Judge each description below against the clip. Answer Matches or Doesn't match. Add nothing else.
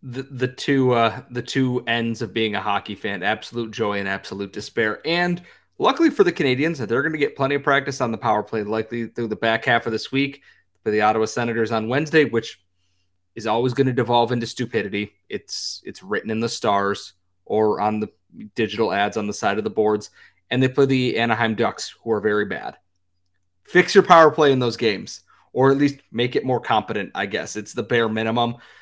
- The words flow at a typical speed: Doesn't match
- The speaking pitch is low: Matches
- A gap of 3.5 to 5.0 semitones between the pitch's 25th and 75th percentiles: Matches